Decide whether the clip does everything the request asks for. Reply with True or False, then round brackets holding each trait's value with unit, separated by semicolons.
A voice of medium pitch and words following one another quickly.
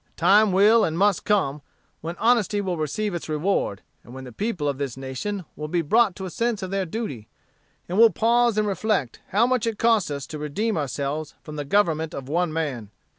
True (180 Hz; 215 wpm)